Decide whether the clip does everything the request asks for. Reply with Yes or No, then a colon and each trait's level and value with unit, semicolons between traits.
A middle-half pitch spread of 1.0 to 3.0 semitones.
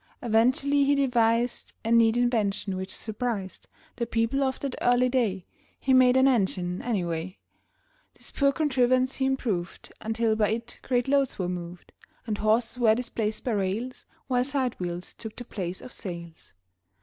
No: average, 4.2 semitones